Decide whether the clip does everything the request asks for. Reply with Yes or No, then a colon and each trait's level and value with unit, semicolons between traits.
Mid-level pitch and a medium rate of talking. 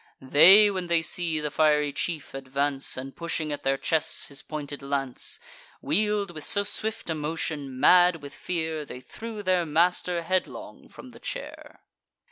Yes: medium, 160 Hz; average, 160 wpm